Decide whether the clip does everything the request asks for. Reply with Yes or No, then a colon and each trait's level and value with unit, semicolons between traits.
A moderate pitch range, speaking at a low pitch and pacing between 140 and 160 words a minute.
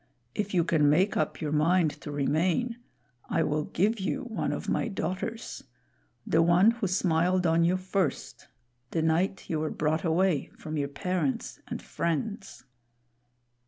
No: average, 3.6 semitones; medium, 175 Hz; average, 155 wpm